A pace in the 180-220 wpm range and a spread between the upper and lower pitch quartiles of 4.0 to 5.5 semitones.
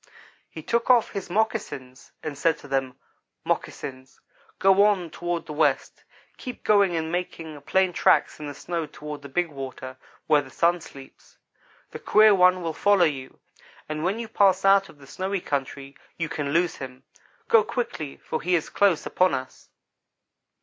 No: average, 170 wpm; average, 5.1 semitones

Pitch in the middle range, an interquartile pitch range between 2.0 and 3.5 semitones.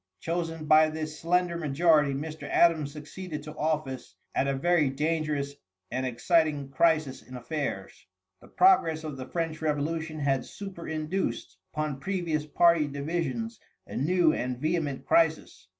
Yes: medium, 155 Hz; average, 2.7 semitones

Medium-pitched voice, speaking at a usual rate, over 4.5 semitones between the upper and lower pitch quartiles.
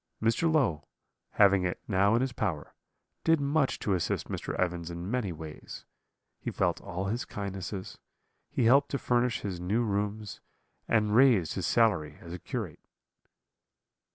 No: low, 105 Hz; average, 155 wpm; average, 5.0 semitones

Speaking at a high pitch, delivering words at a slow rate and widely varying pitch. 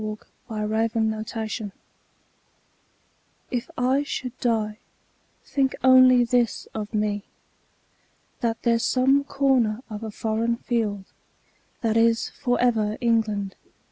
No: high, 230 Hz; slow, 105 wpm; narrow, 2.5 semitones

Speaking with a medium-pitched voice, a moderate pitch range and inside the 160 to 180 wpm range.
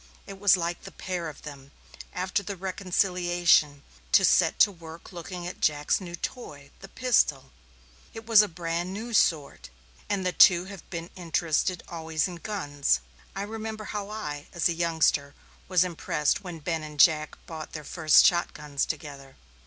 Yes: medium, 175 Hz; average, 3.8 semitones; average, 170 wpm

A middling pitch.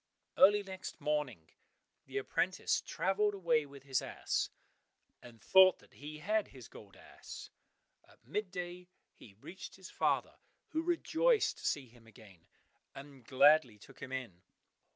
Yes: medium, 150 Hz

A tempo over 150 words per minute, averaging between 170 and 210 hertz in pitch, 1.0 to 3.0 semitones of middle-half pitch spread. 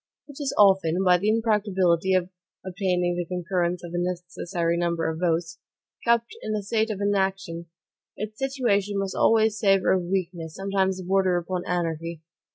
Yes: average, 160 wpm; medium, 185 Hz; average, 2.7 semitones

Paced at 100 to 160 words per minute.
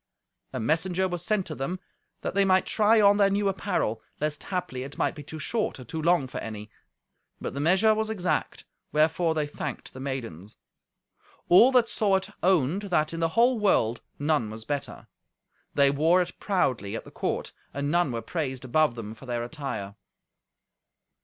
No: average, 185 wpm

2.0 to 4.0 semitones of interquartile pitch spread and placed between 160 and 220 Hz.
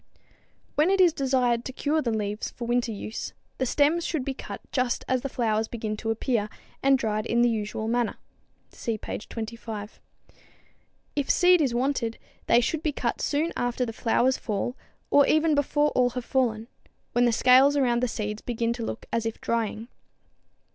No: average, 3.4 semitones; high, 240 Hz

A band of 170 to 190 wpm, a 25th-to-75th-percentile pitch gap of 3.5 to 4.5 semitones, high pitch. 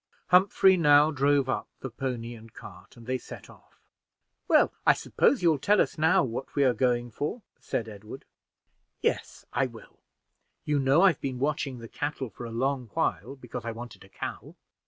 No: average, 180 wpm; average, 3.8 semitones; low, 130 Hz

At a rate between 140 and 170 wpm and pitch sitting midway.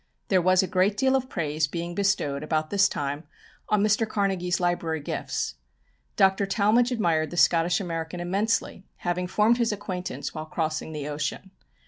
Yes: average, 160 wpm; medium, 180 Hz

